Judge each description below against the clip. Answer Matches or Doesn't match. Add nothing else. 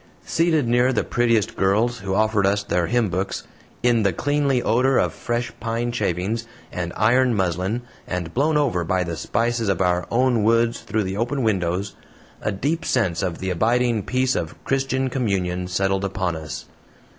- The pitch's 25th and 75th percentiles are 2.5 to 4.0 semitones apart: Doesn't match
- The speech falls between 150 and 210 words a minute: Matches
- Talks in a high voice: Doesn't match